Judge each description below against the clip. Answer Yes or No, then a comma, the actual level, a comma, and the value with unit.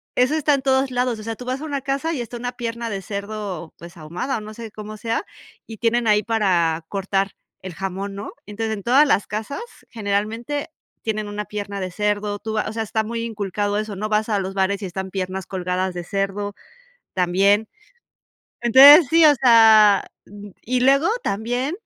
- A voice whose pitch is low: No, high, 215 Hz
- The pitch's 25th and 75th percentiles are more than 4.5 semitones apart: No, average, 3.3 semitones